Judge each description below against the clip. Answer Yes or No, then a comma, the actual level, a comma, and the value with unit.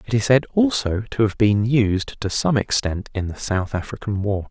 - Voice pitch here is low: Yes, low, 110 Hz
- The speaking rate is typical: No, fast, 215 wpm